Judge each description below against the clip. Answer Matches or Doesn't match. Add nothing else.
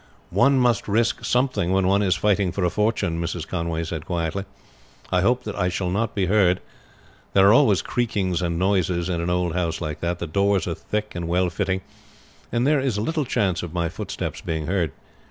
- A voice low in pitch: Matches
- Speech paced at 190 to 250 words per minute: Matches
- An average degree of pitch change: Matches